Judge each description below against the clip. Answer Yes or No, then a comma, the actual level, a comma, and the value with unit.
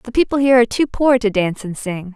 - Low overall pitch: No, high, 230 Hz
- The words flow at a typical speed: No, fast, 280 wpm